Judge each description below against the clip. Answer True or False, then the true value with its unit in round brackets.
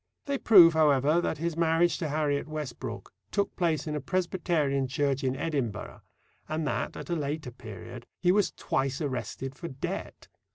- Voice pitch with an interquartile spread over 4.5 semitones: False (3.9 semitones)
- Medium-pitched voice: True (150 Hz)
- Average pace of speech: True (165 wpm)